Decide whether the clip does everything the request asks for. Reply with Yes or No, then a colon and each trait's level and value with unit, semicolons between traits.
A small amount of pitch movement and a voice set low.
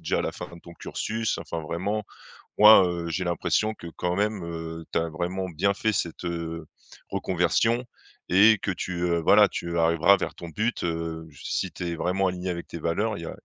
No: average, 3.1 semitones; very low, 85 Hz